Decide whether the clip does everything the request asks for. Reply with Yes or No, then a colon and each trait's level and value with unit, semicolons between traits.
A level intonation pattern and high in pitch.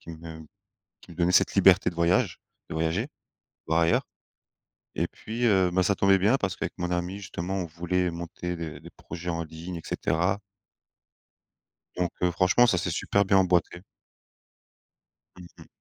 No: narrow, 2.2 semitones; very low, 90 Hz